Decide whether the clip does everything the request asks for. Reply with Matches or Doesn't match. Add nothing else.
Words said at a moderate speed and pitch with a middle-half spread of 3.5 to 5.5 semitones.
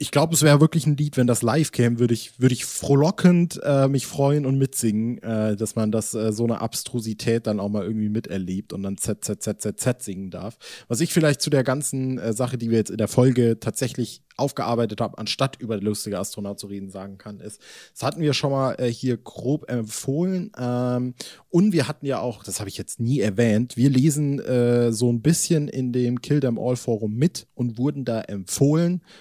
Doesn't match